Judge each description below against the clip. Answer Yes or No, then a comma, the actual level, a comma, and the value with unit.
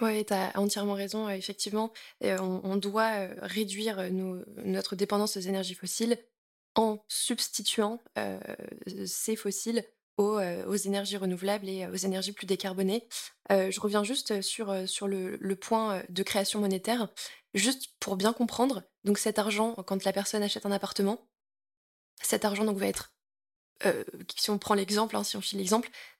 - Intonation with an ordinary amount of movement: No, narrow, 2.1 semitones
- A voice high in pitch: Yes, high, 205 Hz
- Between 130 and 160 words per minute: Yes, average, 155 wpm